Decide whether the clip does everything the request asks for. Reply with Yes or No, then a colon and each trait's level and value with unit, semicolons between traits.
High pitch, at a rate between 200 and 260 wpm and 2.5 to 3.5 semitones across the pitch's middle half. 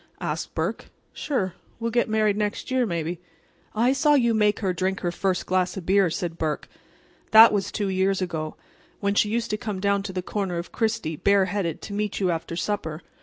Yes: high, 200 Hz; fast, 205 wpm; average, 3.0 semitones